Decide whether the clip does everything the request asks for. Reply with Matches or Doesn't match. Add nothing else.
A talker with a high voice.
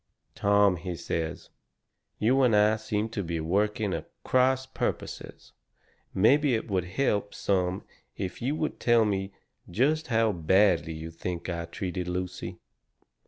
Doesn't match